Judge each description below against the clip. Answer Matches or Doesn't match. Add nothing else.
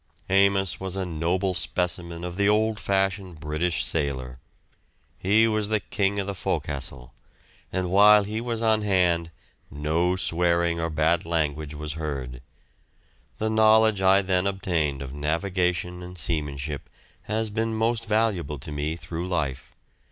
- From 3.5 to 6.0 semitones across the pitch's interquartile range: Matches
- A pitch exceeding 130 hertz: Doesn't match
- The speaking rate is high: Doesn't match